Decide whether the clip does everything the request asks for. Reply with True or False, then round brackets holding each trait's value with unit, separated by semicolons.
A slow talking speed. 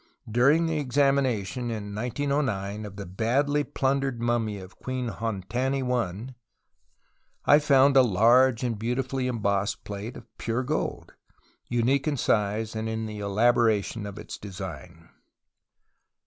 True (125 wpm)